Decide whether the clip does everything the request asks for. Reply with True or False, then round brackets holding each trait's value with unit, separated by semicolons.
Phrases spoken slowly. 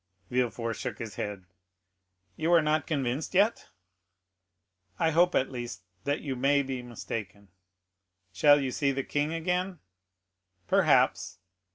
True (130 wpm)